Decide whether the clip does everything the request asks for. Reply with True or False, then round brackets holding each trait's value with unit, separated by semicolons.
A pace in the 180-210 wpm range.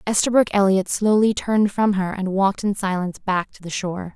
True (200 wpm)